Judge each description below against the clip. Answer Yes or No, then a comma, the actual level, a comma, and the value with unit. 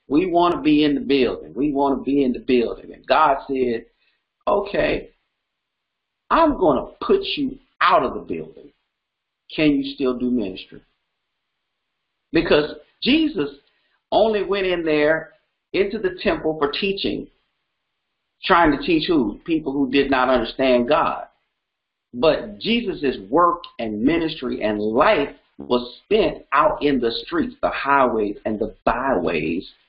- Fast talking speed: No, average, 145 wpm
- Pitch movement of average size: No, wide, 7.6 semitones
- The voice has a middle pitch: Yes, medium, 150 Hz